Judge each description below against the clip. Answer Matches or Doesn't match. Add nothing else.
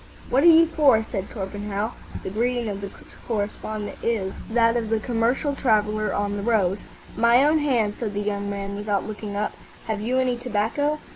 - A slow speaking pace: Doesn't match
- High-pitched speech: Matches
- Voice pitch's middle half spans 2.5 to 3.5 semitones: Matches